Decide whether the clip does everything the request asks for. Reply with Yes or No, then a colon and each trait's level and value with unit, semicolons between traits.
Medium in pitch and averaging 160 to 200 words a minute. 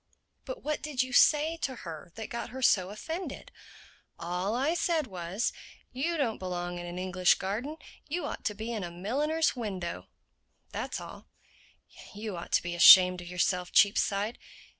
No: high, 210 Hz; average, 165 wpm